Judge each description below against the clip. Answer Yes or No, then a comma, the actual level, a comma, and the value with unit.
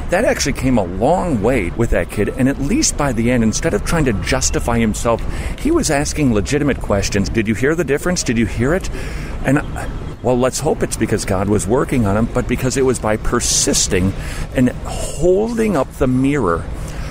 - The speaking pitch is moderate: No, low, 120 Hz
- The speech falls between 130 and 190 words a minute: No, average, 200 wpm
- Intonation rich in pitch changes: No, average, 4.3 semitones